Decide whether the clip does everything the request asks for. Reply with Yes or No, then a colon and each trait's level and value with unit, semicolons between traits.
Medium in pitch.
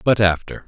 No: low, 100 Hz